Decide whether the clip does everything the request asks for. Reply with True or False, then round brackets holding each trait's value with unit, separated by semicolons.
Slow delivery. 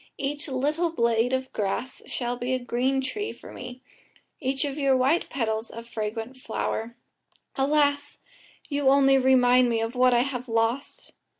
False (160 wpm)